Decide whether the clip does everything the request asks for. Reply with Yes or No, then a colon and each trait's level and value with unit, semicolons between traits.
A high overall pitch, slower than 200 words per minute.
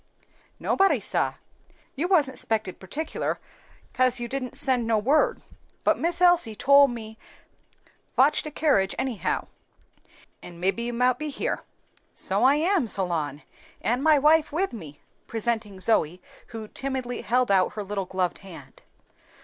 Yes: high, 240 Hz; average, 140 wpm